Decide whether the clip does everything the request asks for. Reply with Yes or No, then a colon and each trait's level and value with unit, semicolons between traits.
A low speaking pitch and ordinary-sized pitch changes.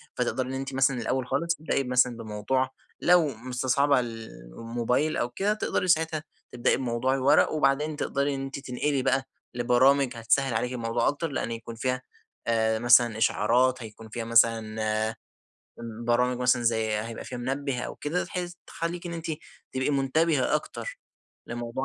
Yes: low, 125 Hz; average, 3.0 semitones